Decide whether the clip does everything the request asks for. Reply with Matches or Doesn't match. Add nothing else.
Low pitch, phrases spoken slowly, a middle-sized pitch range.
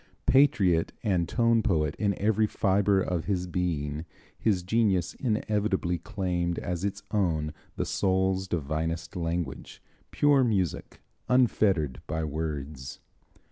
Matches